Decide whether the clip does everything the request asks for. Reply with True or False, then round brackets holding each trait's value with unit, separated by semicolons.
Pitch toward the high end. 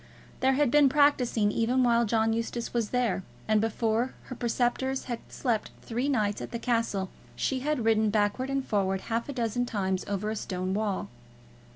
True (230 Hz)